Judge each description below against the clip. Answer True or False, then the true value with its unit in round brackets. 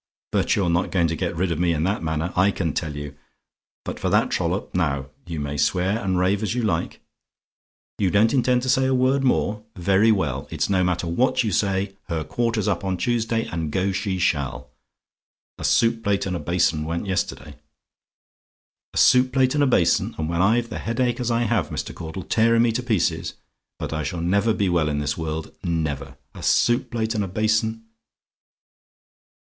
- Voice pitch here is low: True (95 Hz)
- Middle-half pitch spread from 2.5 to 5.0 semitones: False (5.4 semitones)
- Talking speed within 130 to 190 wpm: False (200 wpm)